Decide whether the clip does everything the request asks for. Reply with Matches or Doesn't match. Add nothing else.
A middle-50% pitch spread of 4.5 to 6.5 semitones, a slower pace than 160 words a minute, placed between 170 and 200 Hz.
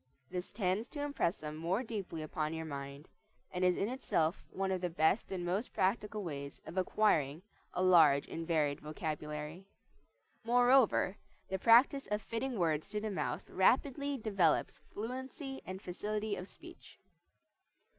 Matches